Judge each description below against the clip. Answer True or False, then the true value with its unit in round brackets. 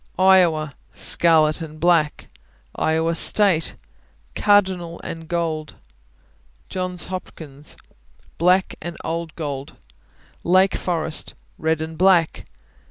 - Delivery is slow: True (95 wpm)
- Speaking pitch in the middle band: True (165 Hz)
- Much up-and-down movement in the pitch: False (2.5 semitones)